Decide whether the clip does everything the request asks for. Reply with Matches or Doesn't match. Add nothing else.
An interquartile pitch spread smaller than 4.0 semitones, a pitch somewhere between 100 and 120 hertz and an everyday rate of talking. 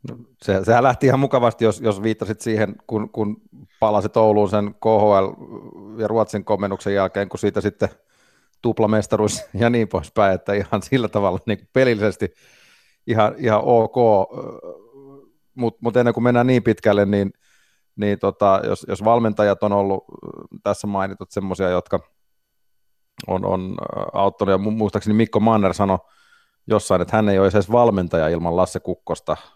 Matches